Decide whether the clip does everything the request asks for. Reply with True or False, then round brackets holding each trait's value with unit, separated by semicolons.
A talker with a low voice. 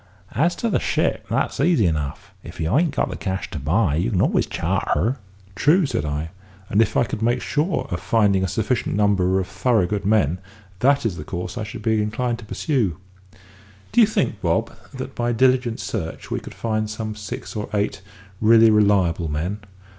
True (105 Hz)